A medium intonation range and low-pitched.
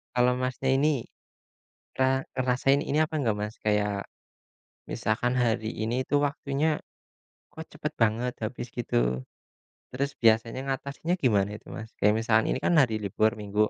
Yes: average, 3.8 semitones; low, 120 Hz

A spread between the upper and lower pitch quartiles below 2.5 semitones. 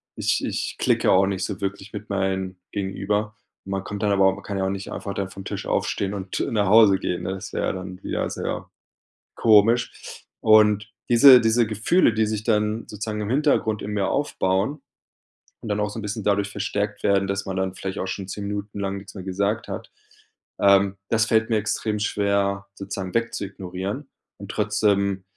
Yes: narrow, 1.8 semitones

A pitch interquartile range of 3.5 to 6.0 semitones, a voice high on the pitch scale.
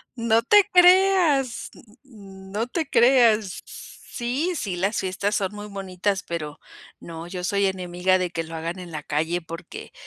Yes: average, 5.3 semitones; high, 195 Hz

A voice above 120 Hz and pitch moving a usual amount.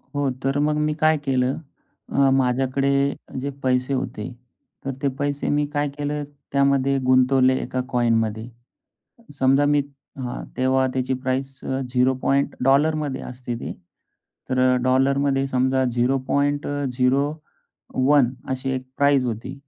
No: low, 135 Hz; narrow, 1.7 semitones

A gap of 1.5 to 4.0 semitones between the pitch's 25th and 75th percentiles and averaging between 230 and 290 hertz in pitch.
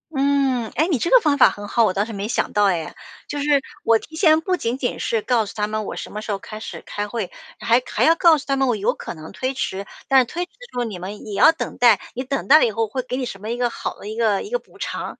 No: average, 5.0 semitones; high, 235 Hz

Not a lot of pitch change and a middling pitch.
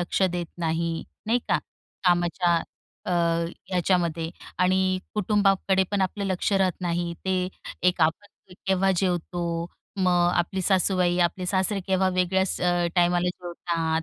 Yes: narrow, 1.5 semitones; medium, 180 Hz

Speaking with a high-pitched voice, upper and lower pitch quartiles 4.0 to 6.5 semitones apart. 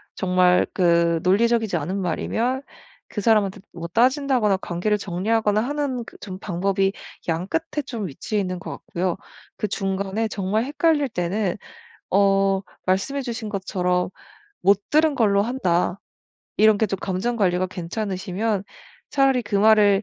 No: high, 200 Hz; average, 3.6 semitones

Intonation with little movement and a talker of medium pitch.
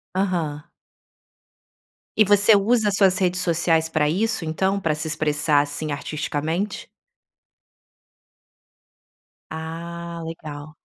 No: average, 3.7 semitones; medium, 165 Hz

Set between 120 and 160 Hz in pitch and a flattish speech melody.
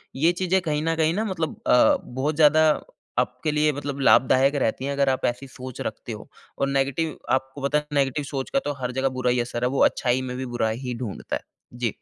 No: low, 135 Hz; average, 3.2 semitones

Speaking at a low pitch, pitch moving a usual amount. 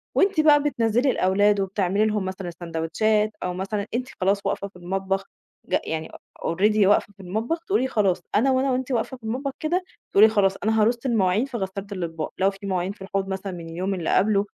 No: high, 200 Hz; average, 3.3 semitones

